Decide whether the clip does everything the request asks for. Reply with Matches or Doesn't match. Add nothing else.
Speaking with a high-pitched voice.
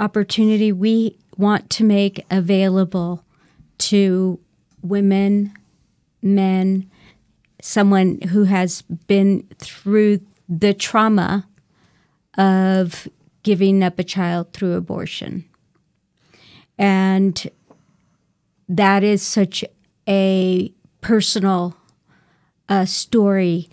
Matches